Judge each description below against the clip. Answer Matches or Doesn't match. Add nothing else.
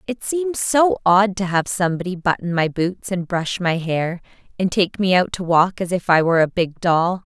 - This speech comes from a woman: Matches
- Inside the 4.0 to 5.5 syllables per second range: Matches